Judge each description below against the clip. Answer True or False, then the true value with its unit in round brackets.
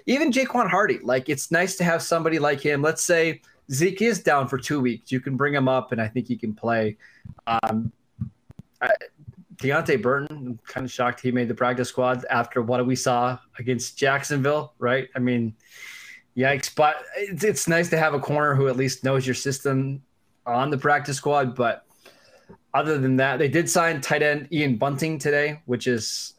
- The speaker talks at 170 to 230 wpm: True (190 wpm)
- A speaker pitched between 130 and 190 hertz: True (135 Hz)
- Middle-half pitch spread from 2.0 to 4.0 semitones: True (3.3 semitones)